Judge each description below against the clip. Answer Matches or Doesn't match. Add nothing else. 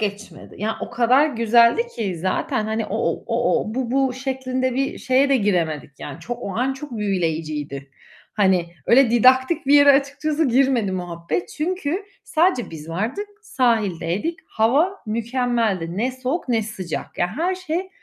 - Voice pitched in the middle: Doesn't match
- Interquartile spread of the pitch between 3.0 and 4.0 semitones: Doesn't match